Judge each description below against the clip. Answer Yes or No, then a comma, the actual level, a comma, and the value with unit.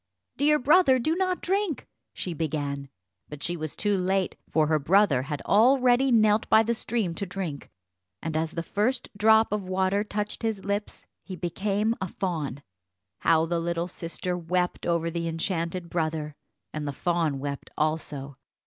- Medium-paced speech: Yes, average, 165 wpm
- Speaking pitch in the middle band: Yes, medium, 180 Hz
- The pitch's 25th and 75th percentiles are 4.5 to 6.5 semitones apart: Yes, average, 4.9 semitones